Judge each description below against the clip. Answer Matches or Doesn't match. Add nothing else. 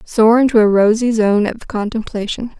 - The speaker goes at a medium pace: Matches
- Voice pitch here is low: Doesn't match